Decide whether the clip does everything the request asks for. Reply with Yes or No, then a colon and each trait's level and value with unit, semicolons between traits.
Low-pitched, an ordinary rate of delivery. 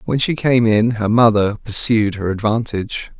Yes: low, 110 Hz; average, 170 wpm